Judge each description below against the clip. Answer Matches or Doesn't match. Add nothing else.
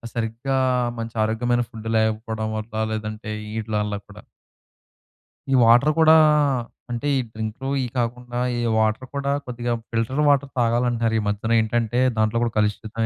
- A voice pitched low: Matches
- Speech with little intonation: Matches